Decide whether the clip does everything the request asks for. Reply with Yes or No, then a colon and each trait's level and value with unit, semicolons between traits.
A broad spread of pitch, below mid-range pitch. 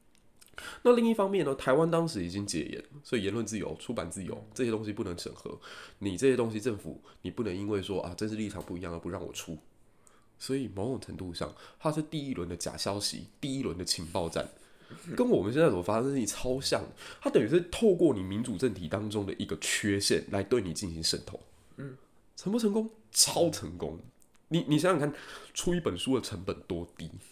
Yes: wide, 7.1 semitones; low, 110 Hz